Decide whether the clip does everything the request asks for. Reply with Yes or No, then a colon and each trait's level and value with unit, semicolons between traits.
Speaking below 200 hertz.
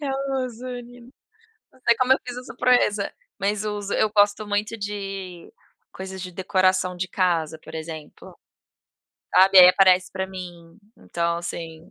Yes: high, 190 Hz